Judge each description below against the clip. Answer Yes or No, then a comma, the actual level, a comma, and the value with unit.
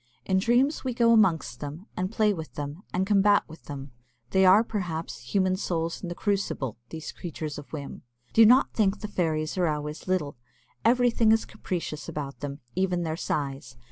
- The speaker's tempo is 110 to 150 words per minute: No, average, 180 wpm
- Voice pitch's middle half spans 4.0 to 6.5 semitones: Yes, wide, 5.5 semitones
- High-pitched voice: No, medium, 180 Hz